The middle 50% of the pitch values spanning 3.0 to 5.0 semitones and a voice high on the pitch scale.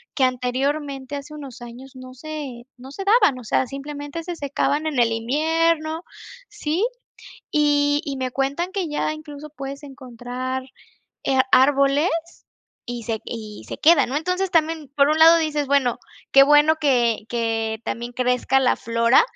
Yes: average, 3.4 semitones; very high, 280 Hz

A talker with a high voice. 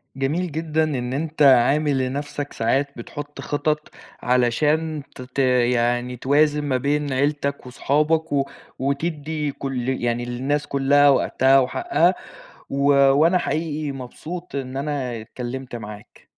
No: medium, 140 Hz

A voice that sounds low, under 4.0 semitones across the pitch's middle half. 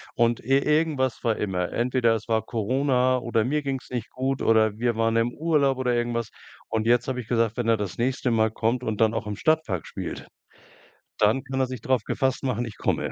Yes: low, 120 Hz; average, 2.7 semitones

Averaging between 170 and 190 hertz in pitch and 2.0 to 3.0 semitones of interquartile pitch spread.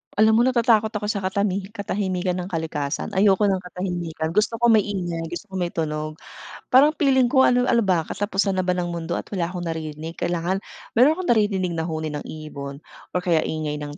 No: medium, 185 Hz; average, 4.3 semitones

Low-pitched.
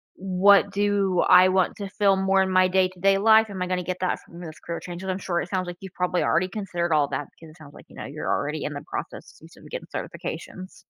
No: medium, 185 Hz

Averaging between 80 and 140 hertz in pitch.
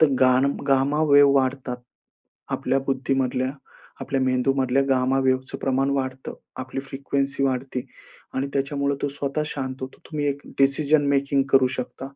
Yes: low, 135 Hz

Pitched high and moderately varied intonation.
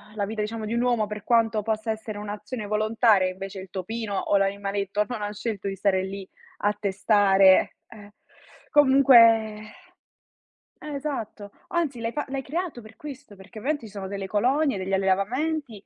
Yes: high, 215 Hz; average, 3.2 semitones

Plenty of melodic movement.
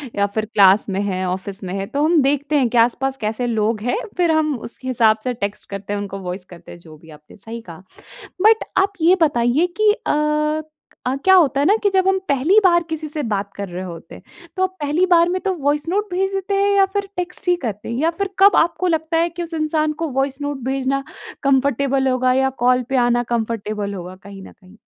Yes: wide, 8.3 semitones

